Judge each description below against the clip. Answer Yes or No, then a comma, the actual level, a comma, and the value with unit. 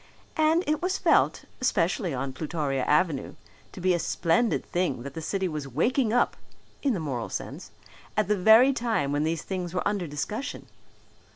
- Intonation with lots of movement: Yes, wide, 6.8 semitones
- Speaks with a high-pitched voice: No, medium, 180 Hz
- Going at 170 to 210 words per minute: Yes, average, 175 wpm